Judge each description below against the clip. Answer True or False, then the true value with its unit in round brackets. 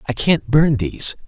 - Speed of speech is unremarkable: True (190 wpm)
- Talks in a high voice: False (150 Hz)